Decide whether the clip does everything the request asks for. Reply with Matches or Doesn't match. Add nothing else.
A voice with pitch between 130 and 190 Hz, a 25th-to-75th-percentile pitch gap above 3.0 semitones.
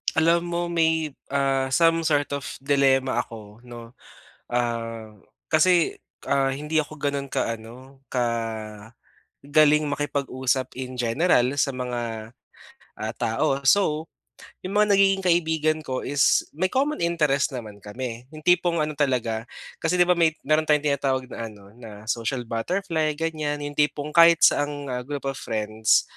Matches